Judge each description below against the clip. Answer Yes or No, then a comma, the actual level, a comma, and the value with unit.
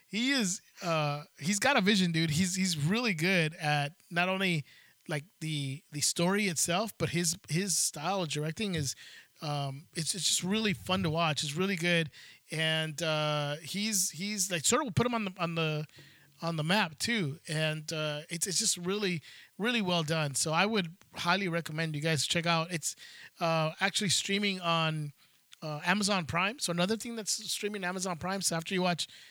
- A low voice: No, medium, 170 Hz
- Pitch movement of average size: Yes, average, 3.7 semitones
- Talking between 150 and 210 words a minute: Yes, average, 190 wpm